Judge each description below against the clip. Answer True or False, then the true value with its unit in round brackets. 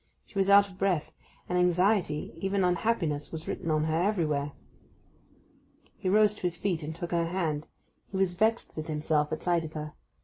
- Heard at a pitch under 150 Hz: False (175 Hz)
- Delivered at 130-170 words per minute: False (190 wpm)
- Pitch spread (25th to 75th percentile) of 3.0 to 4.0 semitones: True (3.7 semitones)